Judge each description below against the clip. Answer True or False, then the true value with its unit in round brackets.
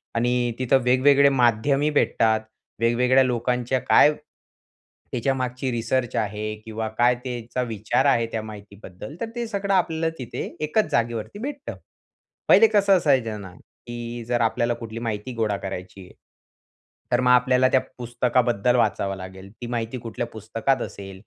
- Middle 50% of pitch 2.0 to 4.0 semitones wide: True (2.9 semitones)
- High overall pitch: False (120 Hz)